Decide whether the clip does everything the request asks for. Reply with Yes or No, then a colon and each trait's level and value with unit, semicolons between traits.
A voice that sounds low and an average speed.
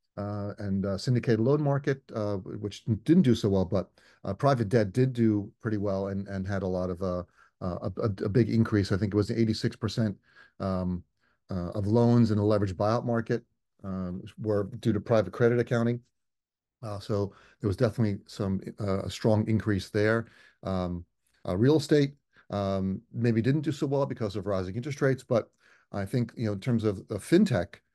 Yes: low, 105 Hz; average, 190 wpm